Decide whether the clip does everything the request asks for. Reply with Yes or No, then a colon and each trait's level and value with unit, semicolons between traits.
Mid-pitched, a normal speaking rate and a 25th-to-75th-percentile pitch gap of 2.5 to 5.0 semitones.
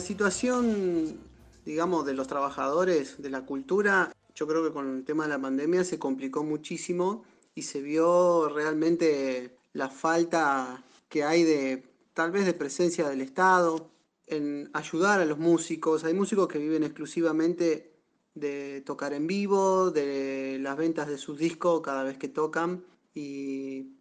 Yes: medium, 155 Hz; average, 150 wpm; average, 3.4 semitones